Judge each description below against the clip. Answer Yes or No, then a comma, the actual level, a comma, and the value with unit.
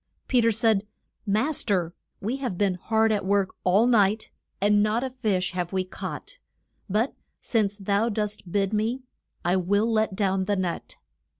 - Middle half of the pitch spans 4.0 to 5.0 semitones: No, average, 2.7 semitones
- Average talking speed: Yes, average, 175 wpm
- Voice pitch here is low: No, high, 205 Hz